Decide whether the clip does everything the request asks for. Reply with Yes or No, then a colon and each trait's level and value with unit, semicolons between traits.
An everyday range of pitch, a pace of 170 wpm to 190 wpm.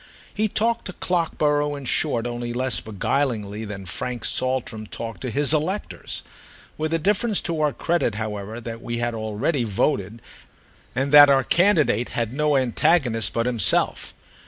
No: average, 5.0 semitones; average, 155 wpm